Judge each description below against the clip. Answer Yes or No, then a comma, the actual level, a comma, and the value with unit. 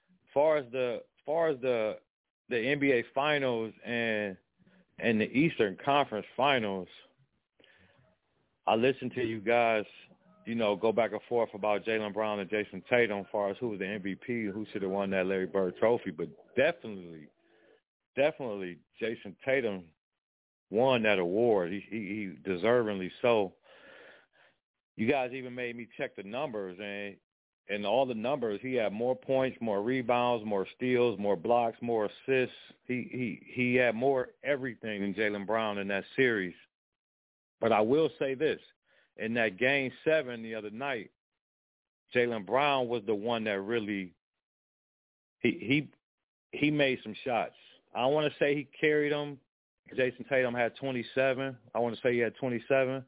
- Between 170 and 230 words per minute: No, average, 160 wpm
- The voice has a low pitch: Yes, low, 115 Hz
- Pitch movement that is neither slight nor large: Yes, average, 3.9 semitones